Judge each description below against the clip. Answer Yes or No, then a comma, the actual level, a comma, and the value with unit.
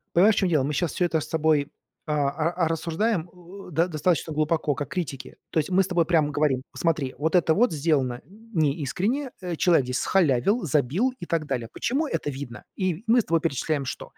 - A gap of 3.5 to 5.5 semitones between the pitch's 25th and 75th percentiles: Yes, average, 3.8 semitones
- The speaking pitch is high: No, medium, 160 Hz